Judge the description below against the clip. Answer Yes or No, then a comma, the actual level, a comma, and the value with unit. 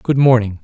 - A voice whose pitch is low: Yes, low, 120 Hz